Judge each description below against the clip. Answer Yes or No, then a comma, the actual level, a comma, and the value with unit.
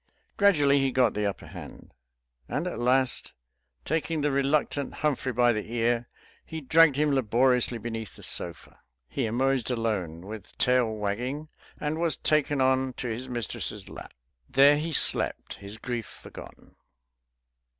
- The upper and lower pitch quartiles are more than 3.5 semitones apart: Yes, average, 4.0 semitones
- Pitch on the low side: Yes, low, 130 Hz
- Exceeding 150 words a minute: No, average, 145 wpm